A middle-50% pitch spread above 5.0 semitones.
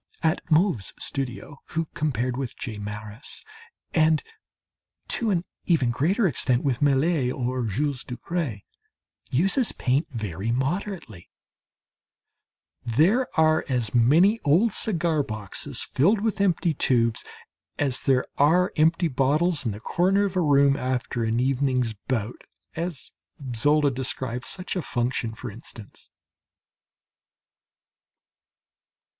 Yes: wide, 5.5 semitones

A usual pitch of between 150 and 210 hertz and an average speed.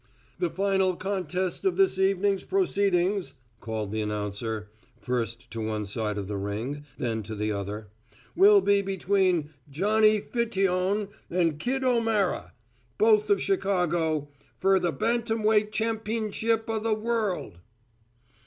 No: high, 190 Hz; slow, 125 wpm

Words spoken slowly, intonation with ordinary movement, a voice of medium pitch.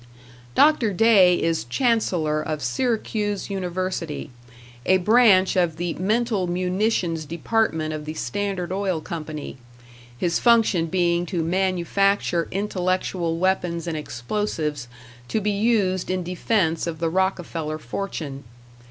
Yes: slow, 115 wpm; average, 3.5 semitones; medium, 180 Hz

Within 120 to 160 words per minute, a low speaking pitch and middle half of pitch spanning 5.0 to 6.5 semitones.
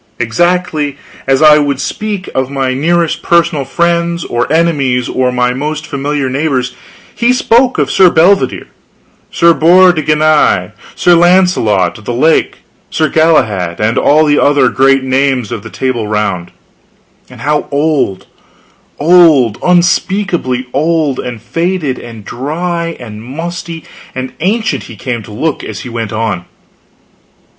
No: average, 140 wpm; medium, 145 Hz; average, 5.3 semitones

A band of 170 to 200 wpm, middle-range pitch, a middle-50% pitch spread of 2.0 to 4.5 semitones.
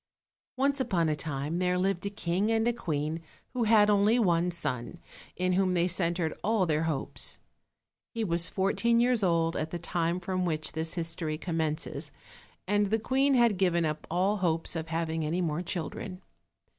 Yes: average, 175 wpm; medium, 175 Hz; average, 3.8 semitones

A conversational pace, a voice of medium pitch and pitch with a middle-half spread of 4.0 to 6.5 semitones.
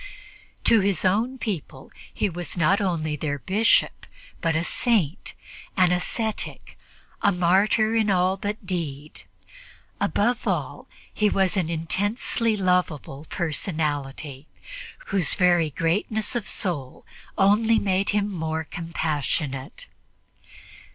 No: slow, 110 wpm; medium, 180 Hz; average, 4.5 semitones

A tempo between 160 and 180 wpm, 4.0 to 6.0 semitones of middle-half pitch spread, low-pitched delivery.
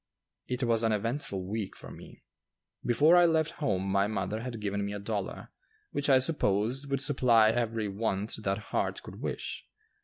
Yes: average, 175 wpm; average, 4.4 semitones; low, 115 Hz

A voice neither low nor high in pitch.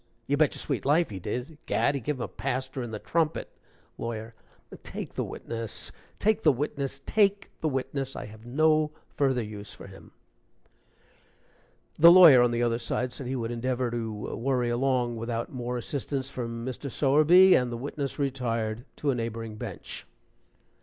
No: low, 125 Hz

